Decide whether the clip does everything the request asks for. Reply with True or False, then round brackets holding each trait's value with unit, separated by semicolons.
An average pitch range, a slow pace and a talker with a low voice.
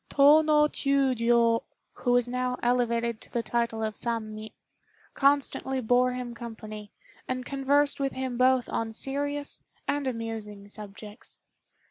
False (3.1 semitones; 130 wpm; 245 Hz)